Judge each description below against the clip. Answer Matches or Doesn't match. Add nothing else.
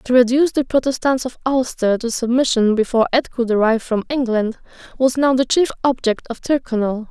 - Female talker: Matches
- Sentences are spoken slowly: Doesn't match